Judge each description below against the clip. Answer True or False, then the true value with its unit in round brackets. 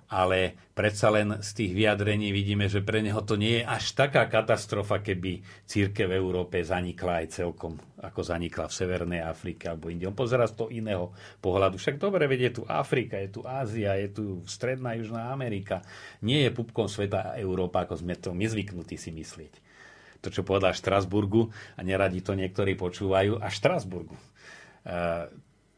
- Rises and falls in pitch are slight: False (3.1 semitones)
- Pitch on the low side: True (100 Hz)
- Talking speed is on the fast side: True (170 wpm)